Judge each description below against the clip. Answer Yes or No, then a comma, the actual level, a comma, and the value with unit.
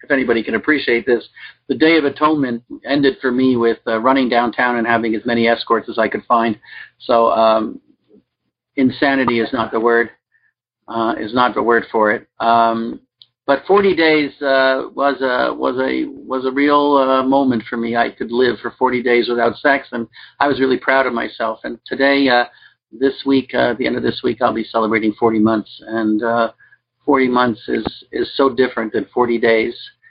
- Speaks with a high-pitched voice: No, low, 125 Hz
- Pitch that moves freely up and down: No, average, 2.7 semitones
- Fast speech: No, average, 195 wpm